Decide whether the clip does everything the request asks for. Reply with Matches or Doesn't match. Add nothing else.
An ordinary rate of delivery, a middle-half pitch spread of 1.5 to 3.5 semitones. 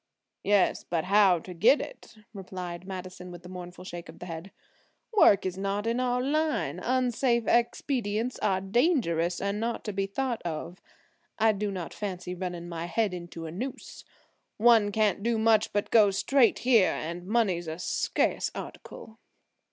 Doesn't match